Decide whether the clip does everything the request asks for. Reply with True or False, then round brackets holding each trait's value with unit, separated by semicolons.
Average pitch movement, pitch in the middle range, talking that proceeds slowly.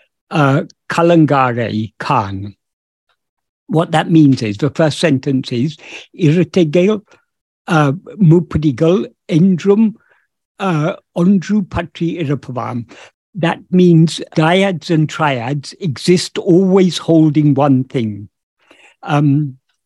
True (4.2 semitones; 160 Hz; 80 wpm)